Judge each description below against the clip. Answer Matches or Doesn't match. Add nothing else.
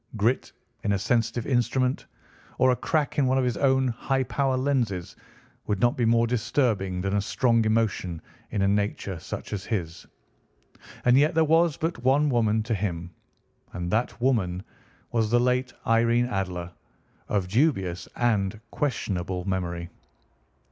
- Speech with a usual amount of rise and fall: Matches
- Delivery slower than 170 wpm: Matches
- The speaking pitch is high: Doesn't match